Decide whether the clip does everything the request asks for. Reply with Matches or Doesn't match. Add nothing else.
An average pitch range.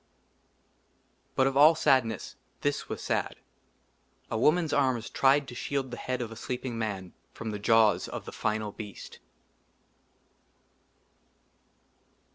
Matches